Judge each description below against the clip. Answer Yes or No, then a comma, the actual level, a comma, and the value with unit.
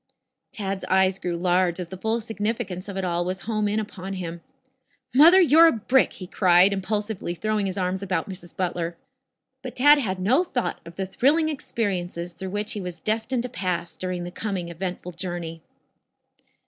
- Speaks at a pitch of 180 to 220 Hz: Yes, high, 190 Hz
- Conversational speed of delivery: Yes, average, 180 wpm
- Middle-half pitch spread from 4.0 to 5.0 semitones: No, average, 3.6 semitones